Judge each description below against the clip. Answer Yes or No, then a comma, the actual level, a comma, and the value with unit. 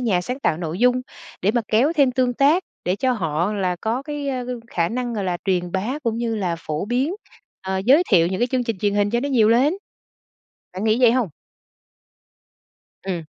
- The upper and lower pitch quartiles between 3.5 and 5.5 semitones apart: Yes, average, 5.1 semitones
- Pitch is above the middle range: Yes, high, 225 Hz